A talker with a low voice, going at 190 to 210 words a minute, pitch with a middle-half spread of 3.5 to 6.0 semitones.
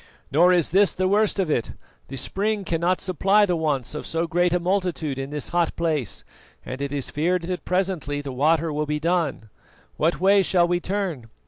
No: medium, 170 Hz; average, 200 wpm; average, 3.8 semitones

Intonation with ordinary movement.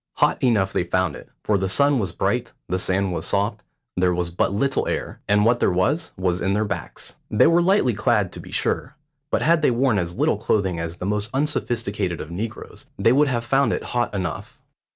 Yes: average, 4.9 semitones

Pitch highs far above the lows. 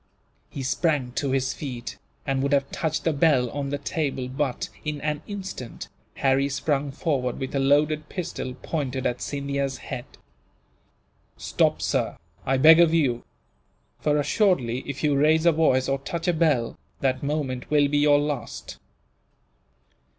No: narrow, 2.5 semitones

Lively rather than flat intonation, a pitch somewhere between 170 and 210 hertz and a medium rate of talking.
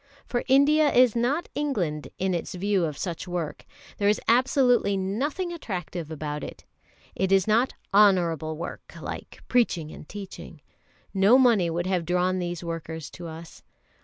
Yes: wide, 6.2 semitones; high, 190 Hz; average, 155 wpm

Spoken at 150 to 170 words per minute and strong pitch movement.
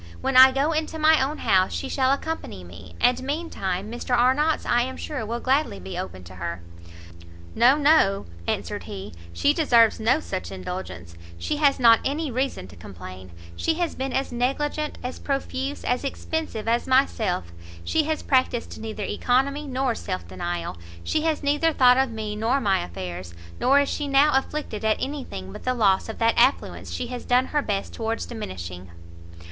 No: average, 185 wpm; wide, 6.7 semitones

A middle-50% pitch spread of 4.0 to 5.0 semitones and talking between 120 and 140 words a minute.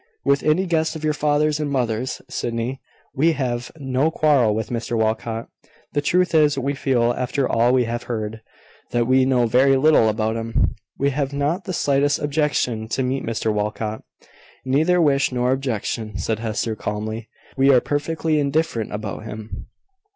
No: average, 4.3 semitones; average, 165 wpm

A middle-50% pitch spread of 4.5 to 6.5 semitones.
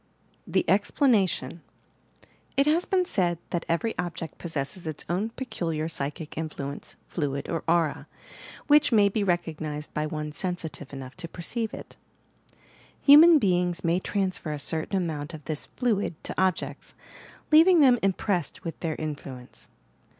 Yes: average, 4.9 semitones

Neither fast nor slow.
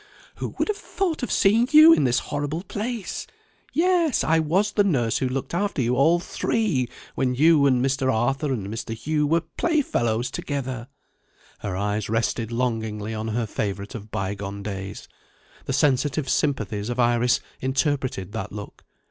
Yes: average, 160 wpm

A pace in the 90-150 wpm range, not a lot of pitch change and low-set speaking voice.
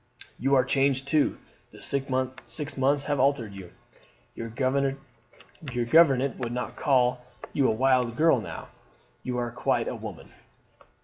Yes: slow, 135 wpm; narrow, 2.1 semitones; low, 130 Hz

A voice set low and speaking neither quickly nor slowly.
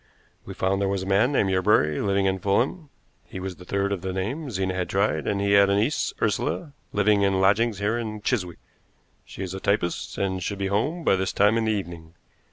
No: low, 100 Hz; fast, 225 wpm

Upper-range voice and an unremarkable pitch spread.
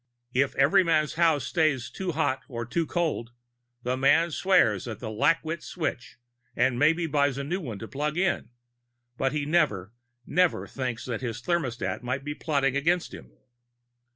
No: medium, 140 Hz; average, 4.9 semitones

